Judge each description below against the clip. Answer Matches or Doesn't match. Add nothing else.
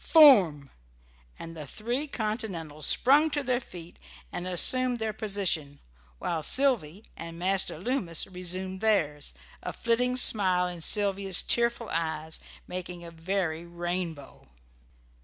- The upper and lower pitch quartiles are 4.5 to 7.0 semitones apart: Matches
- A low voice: Doesn't match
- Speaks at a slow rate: Matches